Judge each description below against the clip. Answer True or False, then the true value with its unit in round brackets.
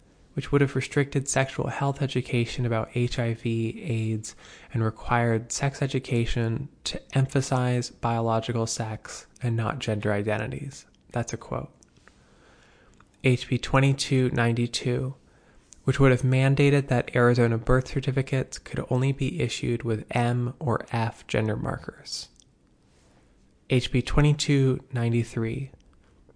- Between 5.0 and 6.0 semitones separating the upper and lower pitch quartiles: False (2.7 semitones)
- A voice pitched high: False (125 Hz)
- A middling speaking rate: False (105 wpm)